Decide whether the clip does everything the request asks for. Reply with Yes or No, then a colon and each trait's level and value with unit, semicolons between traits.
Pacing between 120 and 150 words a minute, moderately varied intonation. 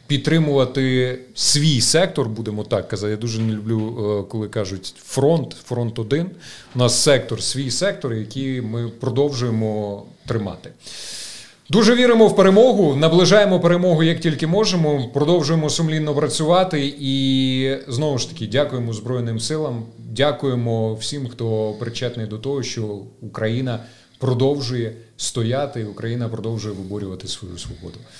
Yes: average, 125 wpm; average, 4.7 semitones